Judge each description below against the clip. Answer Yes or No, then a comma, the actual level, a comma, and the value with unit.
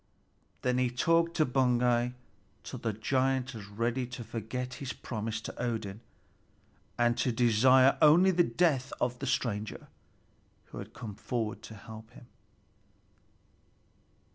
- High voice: No, low, 125 Hz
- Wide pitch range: No, average, 2.7 semitones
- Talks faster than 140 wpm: No, slow, 135 wpm